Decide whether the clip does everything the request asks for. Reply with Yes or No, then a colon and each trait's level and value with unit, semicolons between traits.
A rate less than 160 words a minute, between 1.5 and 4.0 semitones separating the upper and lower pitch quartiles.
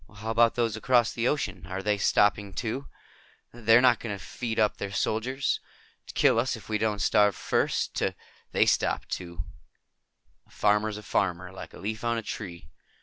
No: average, 195 wpm; narrow, 2.5 semitones